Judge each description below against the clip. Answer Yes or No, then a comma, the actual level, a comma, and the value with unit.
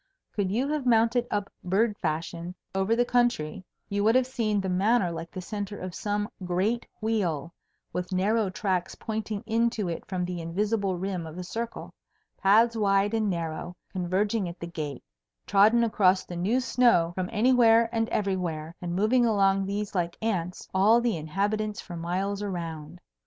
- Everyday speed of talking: Yes, average, 170 wpm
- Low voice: No, high, 195 Hz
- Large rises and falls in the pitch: No, average, 3.9 semitones